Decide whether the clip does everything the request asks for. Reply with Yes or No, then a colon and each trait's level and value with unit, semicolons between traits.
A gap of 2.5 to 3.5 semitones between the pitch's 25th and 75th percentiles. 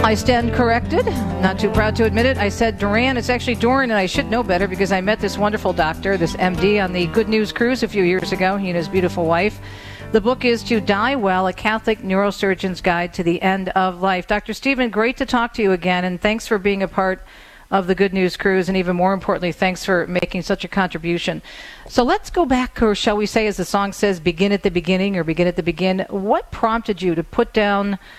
Yes: average, 3.1 semitones